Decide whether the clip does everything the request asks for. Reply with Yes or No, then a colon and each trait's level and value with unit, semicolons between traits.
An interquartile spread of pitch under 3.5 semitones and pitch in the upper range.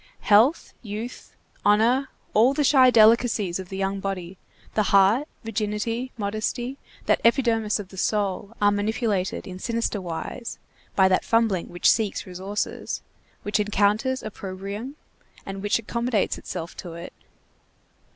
Yes: average, 3.1 semitones; high, 210 Hz